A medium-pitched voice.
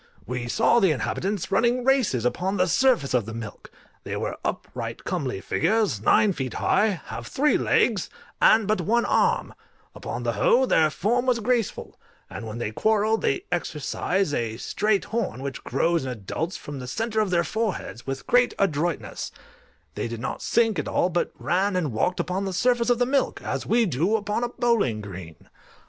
Yes: medium, 180 Hz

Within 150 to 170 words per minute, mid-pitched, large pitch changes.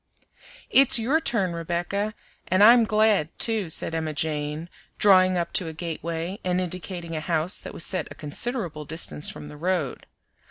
No: average, 165 wpm; medium, 175 Hz; average, 4.0 semitones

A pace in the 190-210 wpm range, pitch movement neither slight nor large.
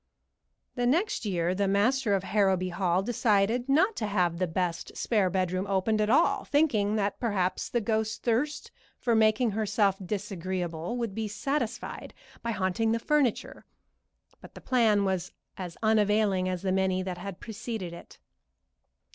No: average, 155 wpm; average, 3.6 semitones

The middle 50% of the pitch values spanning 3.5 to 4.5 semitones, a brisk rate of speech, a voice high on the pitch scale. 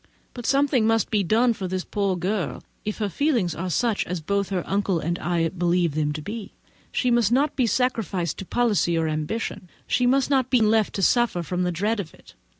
No: average, 5.1 semitones; fast, 220 wpm; high, 200 Hz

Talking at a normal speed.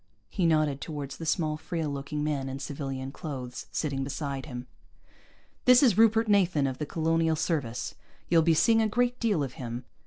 Yes: average, 180 wpm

